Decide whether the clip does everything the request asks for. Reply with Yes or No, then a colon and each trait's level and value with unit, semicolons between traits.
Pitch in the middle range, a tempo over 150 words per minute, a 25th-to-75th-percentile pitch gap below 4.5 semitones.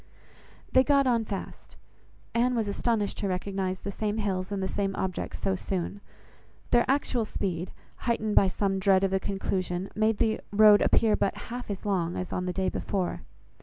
No: high, 200 Hz; average, 180 wpm; narrow, 2.5 semitones